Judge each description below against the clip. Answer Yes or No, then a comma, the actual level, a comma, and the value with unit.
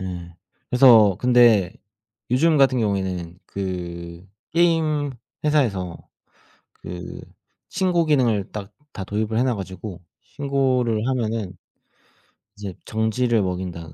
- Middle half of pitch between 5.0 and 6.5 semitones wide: Yes, wide, 5.6 semitones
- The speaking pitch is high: No, low, 110 Hz